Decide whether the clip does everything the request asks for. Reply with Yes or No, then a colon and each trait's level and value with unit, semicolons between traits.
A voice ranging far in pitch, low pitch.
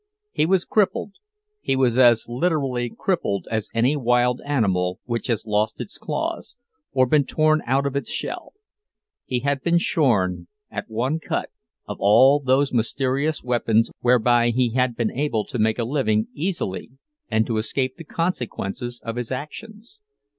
No: average, 4.5 semitones; low, 125 Hz